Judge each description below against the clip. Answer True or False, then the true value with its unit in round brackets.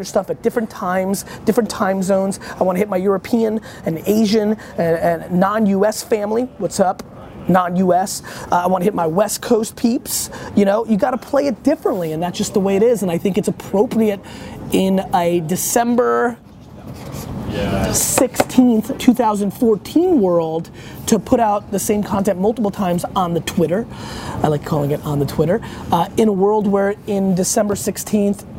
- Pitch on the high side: True (200 Hz)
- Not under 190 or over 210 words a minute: False (180 wpm)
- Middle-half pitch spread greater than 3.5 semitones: False (3.2 semitones)